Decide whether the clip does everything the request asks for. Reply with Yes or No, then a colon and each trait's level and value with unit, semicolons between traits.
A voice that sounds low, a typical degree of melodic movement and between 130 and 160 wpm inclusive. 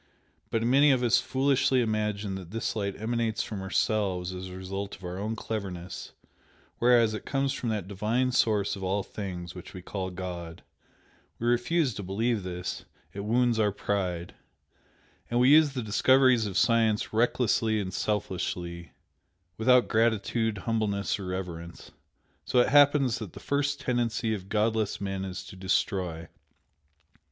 Yes: low, 105 Hz; average, 4.1 semitones; average, 155 wpm